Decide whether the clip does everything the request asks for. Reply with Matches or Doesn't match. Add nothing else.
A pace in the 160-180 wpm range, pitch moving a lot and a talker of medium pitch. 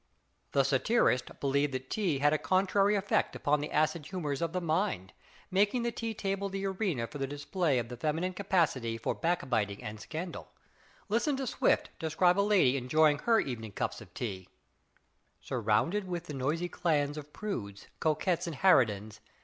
Matches